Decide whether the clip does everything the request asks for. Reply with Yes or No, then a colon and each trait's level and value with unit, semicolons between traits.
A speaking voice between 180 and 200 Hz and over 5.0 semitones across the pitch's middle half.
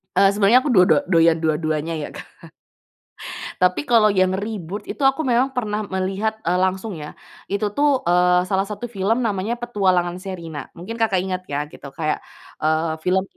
No: high, 190 Hz; average, 3.8 semitones